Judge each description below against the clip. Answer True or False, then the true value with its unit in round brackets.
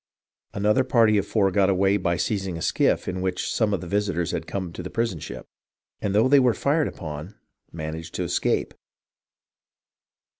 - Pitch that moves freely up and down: False (3.7 semitones)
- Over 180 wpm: False (165 wpm)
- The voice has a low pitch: True (95 Hz)